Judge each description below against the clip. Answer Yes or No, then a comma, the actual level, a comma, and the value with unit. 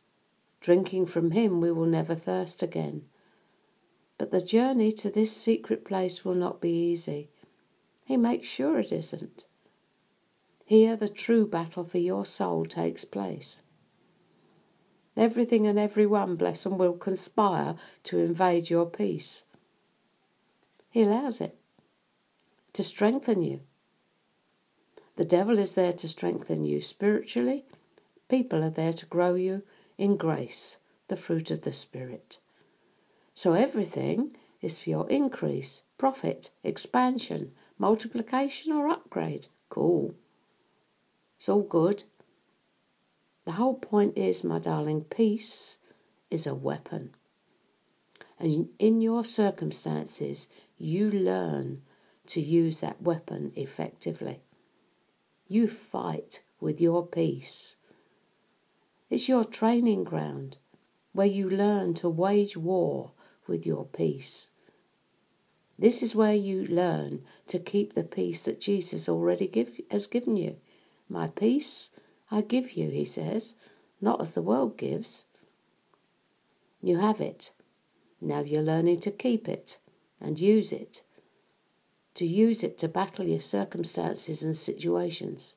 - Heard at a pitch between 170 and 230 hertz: Yes, medium, 185 Hz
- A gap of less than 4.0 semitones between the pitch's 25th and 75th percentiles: No, average, 4.8 semitones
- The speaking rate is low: Yes, slow, 120 wpm